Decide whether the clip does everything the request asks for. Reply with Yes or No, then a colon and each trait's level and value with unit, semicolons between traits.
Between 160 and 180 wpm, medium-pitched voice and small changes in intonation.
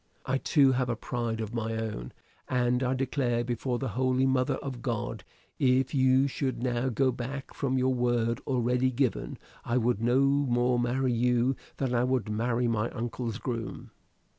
No: average, 170 wpm; low, 125 Hz; narrow, 1.7 semitones